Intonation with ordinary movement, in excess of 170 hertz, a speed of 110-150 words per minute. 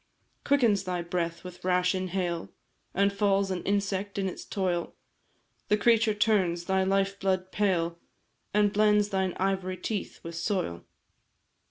No: narrow, 2.0 semitones; high, 190 Hz; average, 140 wpm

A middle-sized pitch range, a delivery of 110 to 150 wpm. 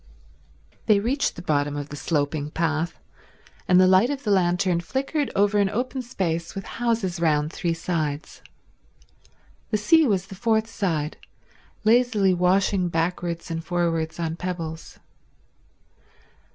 Yes: average, 4.4 semitones; slow, 135 wpm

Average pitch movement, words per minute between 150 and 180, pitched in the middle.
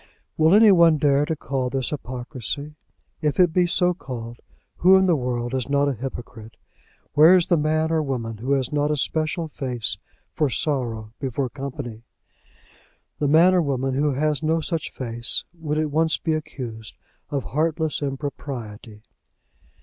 Yes: average, 4.0 semitones; average, 165 wpm; medium, 145 Hz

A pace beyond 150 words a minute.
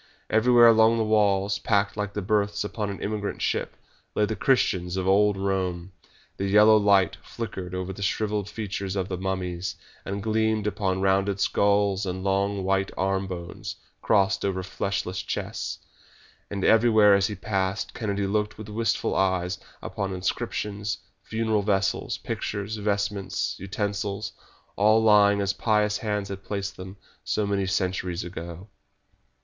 No: average, 145 wpm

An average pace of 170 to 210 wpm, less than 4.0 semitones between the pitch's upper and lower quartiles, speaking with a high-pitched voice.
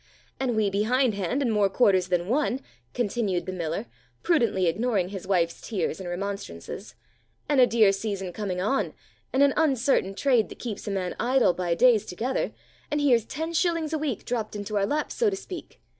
No: average, 185 wpm; wide, 5.5 semitones; high, 215 Hz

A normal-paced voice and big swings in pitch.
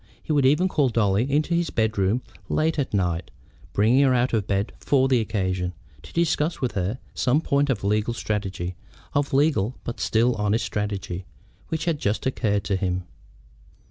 Yes: average, 175 wpm; wide, 5.9 semitones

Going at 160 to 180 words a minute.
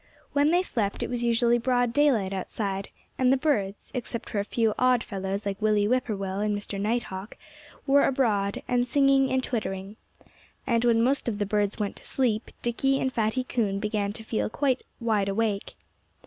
No: average, 190 wpm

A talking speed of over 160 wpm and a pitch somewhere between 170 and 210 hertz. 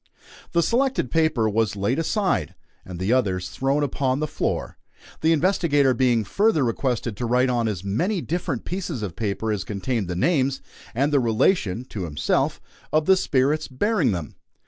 No: average, 170 wpm; low, 130 Hz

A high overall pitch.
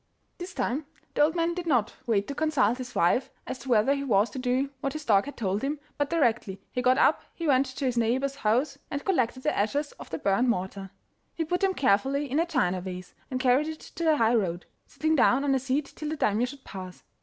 Yes: very high, 260 Hz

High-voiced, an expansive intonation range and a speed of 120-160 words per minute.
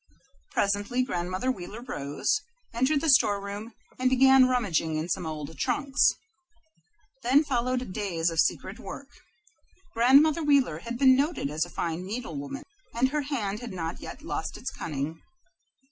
Yes: high, 225 Hz; wide, 7.4 semitones; average, 145 wpm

